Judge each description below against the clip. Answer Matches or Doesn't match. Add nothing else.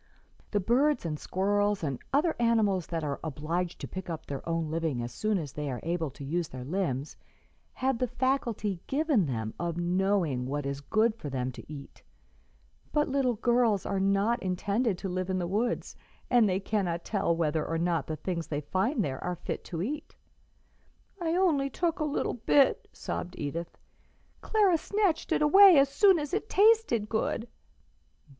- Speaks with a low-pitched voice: Doesn't match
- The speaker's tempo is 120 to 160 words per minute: Doesn't match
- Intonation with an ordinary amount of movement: Doesn't match